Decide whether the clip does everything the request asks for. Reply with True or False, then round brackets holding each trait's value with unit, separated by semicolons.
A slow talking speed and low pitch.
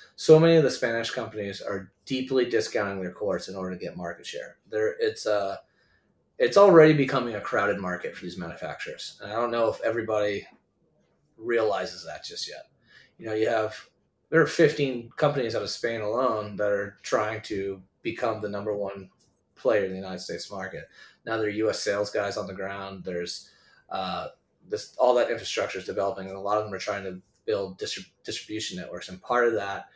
False (200 wpm; 105 Hz)